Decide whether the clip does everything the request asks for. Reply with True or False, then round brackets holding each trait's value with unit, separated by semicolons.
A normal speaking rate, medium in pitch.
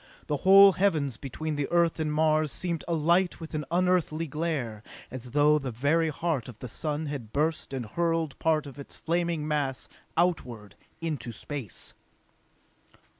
True (155 wpm; 155 Hz)